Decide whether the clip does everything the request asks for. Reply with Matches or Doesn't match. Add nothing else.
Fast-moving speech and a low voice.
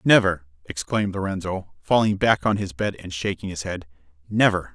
Doesn't match